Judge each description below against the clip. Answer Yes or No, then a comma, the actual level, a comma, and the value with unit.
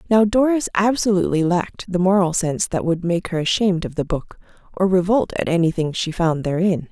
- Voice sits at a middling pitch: Yes, medium, 180 Hz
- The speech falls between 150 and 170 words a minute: No, average, 190 wpm